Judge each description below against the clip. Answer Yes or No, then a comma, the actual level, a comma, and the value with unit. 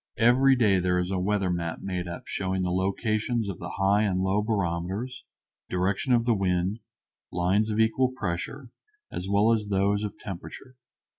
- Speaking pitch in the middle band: No, low, 100 Hz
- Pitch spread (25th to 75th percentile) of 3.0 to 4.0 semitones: Yes, average, 3.4 semitones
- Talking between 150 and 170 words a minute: Yes, average, 165 wpm